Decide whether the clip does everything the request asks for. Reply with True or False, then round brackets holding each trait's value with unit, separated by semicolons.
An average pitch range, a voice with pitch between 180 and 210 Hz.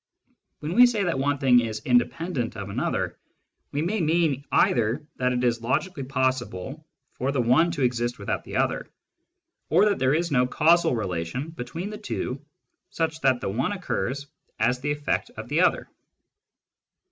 False (4.8 semitones; 135 Hz)